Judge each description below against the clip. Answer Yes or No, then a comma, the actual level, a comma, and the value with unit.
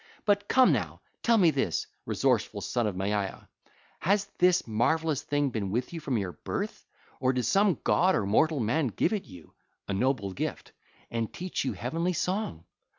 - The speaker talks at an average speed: Yes, average, 165 wpm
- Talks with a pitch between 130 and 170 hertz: Yes, medium, 140 Hz